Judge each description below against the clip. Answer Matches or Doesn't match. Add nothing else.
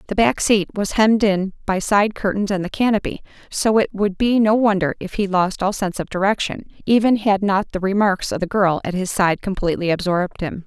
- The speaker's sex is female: Matches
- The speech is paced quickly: Matches